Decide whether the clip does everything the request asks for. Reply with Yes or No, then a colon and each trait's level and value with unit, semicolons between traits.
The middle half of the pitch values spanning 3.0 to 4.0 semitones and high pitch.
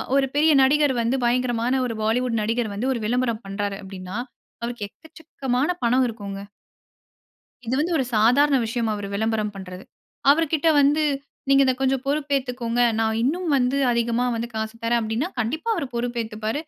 Yes: average, 3.7 semitones; high, 240 Hz